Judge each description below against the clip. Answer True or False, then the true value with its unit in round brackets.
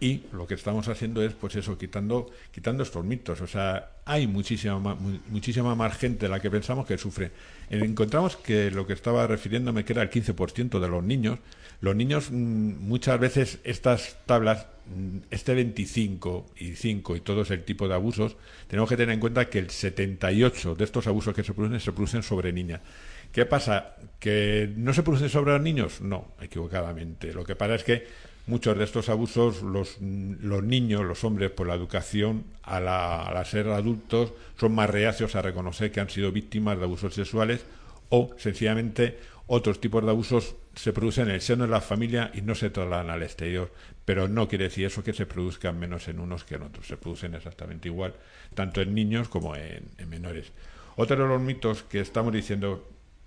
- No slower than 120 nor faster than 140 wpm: False (190 wpm)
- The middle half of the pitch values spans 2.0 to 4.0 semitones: True (3.6 semitones)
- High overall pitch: False (105 Hz)